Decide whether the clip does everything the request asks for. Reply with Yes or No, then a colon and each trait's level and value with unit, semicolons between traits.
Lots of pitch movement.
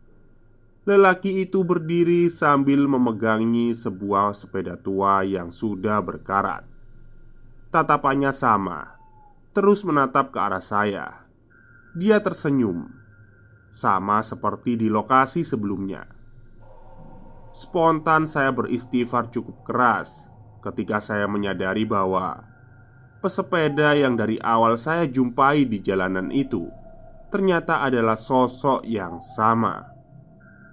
No: average, 4.7 semitones